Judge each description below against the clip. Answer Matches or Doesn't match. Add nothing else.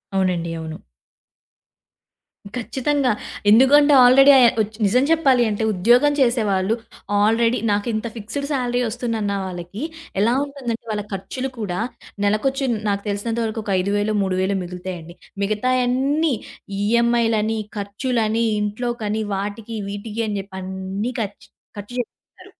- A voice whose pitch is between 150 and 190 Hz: Doesn't match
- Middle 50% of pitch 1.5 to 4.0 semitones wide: Matches